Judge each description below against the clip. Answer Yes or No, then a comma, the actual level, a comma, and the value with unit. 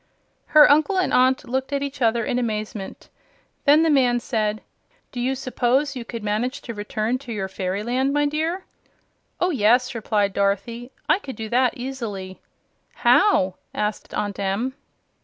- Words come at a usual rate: Yes, average, 155 wpm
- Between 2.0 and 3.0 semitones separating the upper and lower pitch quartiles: No, average, 4.3 semitones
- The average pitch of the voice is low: No, high, 245 Hz